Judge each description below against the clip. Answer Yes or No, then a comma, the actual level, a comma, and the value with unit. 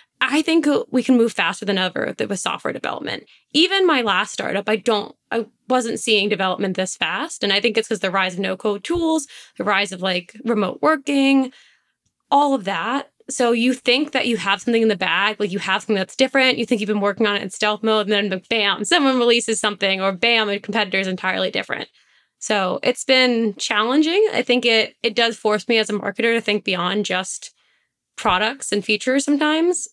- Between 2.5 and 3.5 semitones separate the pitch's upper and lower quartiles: No, average, 4.2 semitones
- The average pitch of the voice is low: No, high, 225 Hz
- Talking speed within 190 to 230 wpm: Yes, fast, 205 wpm